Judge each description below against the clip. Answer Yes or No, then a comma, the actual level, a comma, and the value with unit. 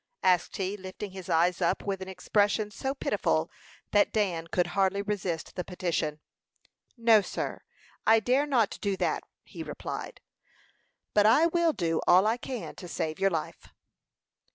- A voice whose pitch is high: Yes, high, 195 Hz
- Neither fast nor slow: Yes, average, 155 wpm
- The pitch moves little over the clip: No, average, 3.4 semitones